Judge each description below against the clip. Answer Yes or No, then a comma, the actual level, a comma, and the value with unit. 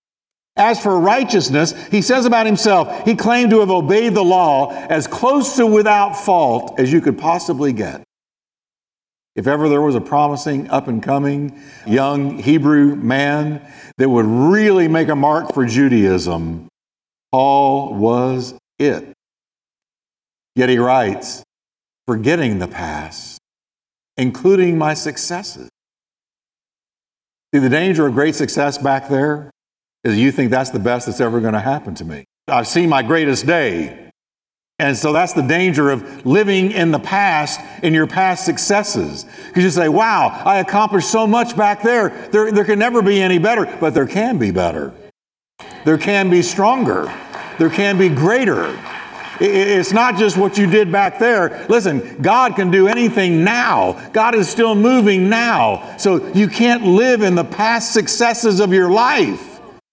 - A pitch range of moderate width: No, wide, 6.7 semitones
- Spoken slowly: No, average, 155 wpm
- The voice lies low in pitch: No, medium, 170 Hz